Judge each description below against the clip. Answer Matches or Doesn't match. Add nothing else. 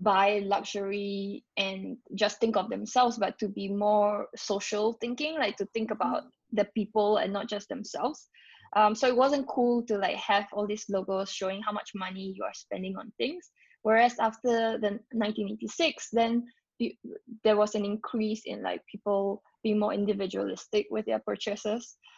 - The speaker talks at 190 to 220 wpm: Doesn't match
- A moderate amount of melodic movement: Doesn't match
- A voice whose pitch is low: Doesn't match